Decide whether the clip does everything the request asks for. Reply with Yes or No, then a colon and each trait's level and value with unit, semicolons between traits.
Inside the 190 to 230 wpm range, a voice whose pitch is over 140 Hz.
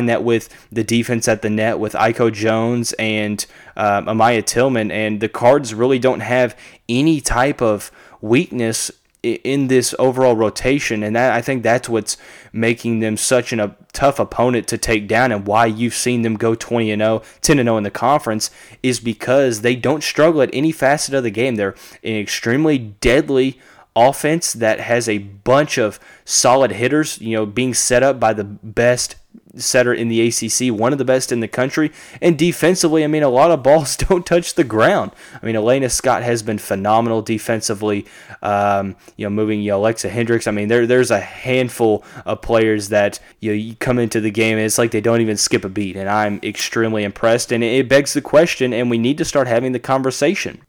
No: average, 200 wpm; low, 115 Hz